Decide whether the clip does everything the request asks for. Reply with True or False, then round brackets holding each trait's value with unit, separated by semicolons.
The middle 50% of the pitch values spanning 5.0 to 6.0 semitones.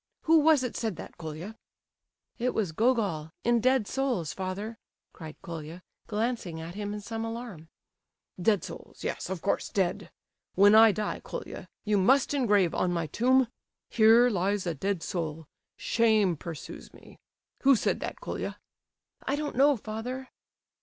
True (5.4 semitones)